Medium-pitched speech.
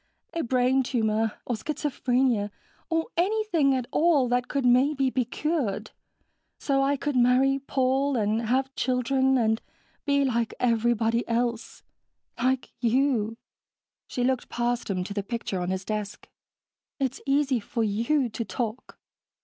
No: very high, 250 Hz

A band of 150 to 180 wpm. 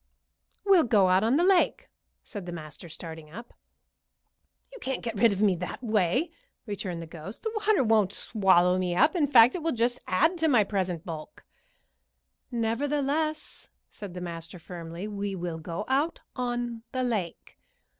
Yes: average, 165 wpm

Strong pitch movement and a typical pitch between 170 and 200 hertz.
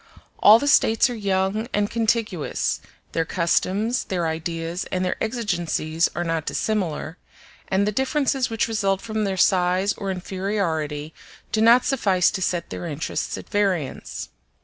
No: average, 4.2 semitones; high, 190 Hz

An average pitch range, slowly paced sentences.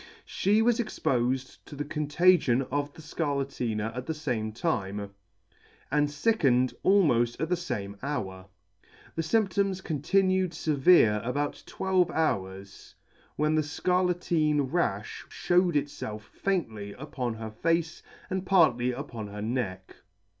No: wide, 6.9 semitones; slow, 125 wpm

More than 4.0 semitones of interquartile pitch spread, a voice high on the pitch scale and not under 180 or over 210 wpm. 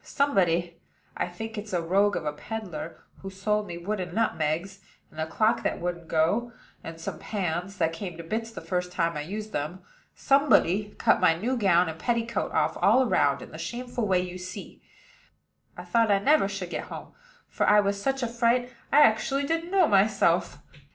Yes: average, 4.9 semitones; high, 195 Hz; average, 190 wpm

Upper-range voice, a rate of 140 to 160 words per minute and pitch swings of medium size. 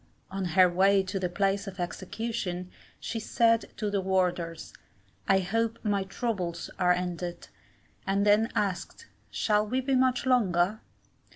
Yes: high, 195 Hz; average, 145 wpm; average, 3.4 semitones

